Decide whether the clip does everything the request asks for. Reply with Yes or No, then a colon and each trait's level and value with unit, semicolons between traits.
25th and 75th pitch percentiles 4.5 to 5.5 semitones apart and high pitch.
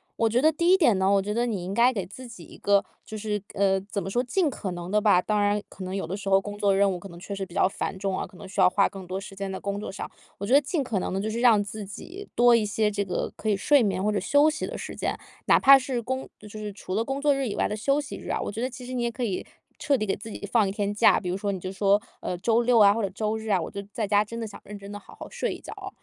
No: average, 3.5 semitones; high, 205 Hz